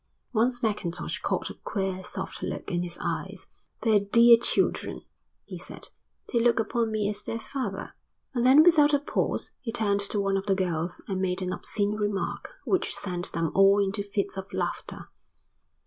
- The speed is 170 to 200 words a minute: Yes, average, 180 wpm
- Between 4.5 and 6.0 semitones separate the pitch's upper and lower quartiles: No, average, 3.4 semitones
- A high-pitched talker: Yes, high, 205 Hz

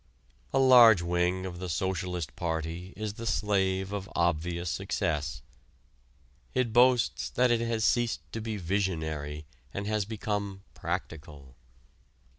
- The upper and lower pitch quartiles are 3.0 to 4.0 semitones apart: No, average, 4.4 semitones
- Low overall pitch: Yes, very low, 95 Hz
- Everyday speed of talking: No, slow, 125 wpm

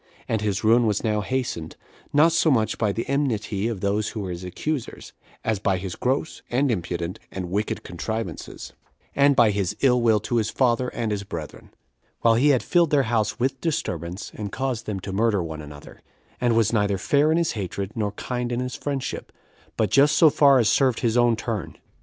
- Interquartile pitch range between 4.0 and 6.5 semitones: Yes, average, 4.6 semitones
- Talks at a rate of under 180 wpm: No, average, 200 wpm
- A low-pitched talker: Yes, low, 115 Hz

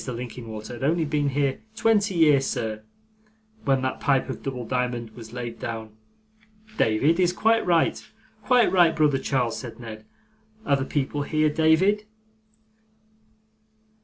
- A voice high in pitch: No, low, 135 Hz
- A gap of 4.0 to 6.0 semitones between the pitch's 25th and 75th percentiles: Yes, average, 5.2 semitones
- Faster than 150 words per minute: No, slow, 135 wpm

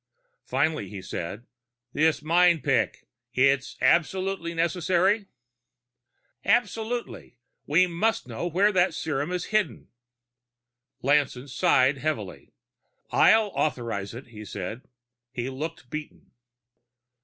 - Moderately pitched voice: Yes, medium, 155 Hz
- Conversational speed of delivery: No, slow, 100 wpm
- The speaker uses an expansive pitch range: Yes, wide, 6.0 semitones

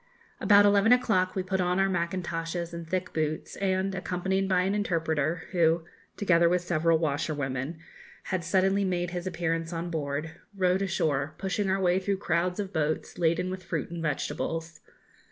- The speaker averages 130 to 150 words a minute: No, average, 165 wpm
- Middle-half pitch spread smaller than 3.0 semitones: Yes, narrow, 2.5 semitones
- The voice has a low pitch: No, medium, 175 Hz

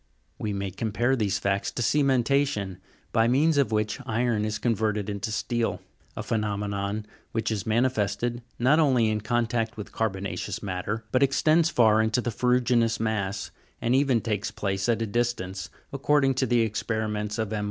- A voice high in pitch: No, low, 110 Hz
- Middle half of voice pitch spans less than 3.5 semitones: Yes, average, 2.8 semitones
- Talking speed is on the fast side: No, average, 165 wpm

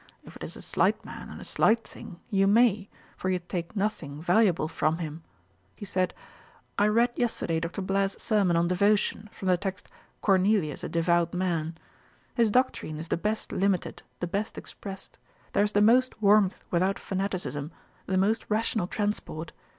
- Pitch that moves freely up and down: No, average, 3.5 semitones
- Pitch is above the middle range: Yes, high, 195 Hz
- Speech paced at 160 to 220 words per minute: Yes, average, 170 wpm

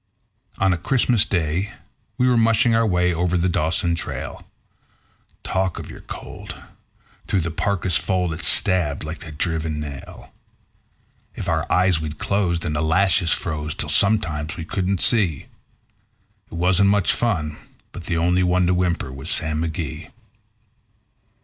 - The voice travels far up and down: No, average, 3.2 semitones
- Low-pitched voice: Yes, very low, 85 Hz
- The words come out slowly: No, average, 150 wpm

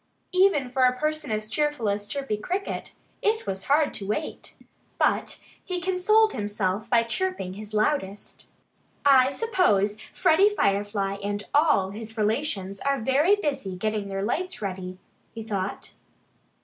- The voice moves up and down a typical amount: No, wide, 7.0 semitones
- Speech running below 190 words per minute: Yes, average, 140 wpm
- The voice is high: Yes, high, 225 Hz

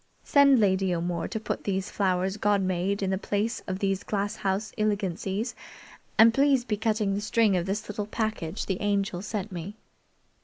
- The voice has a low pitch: No, high, 200 Hz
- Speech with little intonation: Yes, narrow, 2.2 semitones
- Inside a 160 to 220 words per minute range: Yes, average, 180 wpm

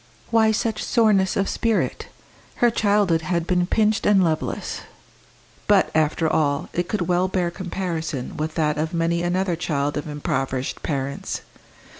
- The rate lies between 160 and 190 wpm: No, average, 145 wpm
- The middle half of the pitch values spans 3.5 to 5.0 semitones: Yes, average, 3.8 semitones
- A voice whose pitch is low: No, medium, 175 Hz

